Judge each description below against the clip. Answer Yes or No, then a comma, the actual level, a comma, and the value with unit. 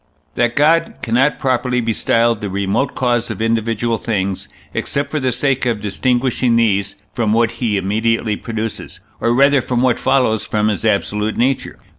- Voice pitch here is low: Yes, low, 115 Hz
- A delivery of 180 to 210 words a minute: No, average, 165 wpm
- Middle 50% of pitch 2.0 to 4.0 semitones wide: Yes, average, 2.8 semitones